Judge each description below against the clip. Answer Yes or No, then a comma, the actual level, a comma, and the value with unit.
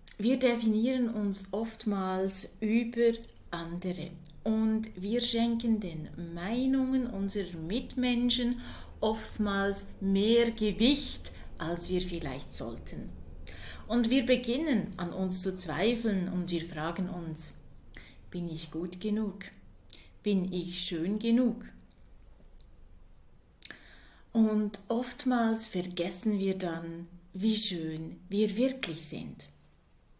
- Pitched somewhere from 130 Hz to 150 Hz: No, high, 200 Hz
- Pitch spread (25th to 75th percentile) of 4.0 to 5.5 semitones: Yes, average, 5.0 semitones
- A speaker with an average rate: No, slow, 95 wpm